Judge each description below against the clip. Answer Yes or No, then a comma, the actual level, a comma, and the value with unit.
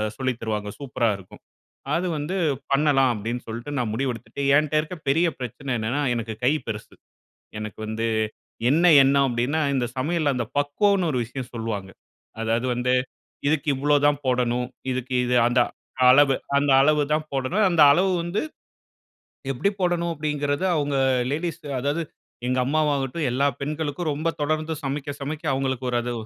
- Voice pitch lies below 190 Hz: Yes, medium, 140 Hz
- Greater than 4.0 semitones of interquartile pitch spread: No, average, 3.7 semitones